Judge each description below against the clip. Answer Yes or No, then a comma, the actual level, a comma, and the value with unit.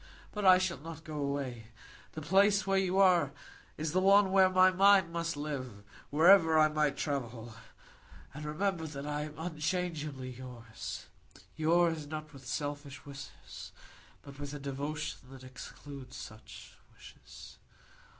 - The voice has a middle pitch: Yes, medium, 150 Hz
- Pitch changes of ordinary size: Yes, average, 4.2 semitones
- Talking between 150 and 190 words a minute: No, average, 140 wpm